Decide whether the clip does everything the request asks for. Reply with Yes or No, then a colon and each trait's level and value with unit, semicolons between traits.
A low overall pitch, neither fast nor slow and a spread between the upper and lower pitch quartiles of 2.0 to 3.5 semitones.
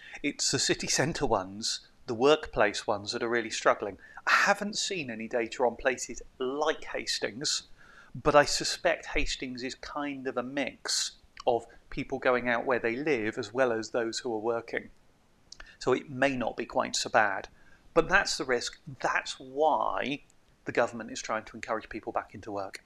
No: low, 120 Hz; average, 180 wpm; average, 4.1 semitones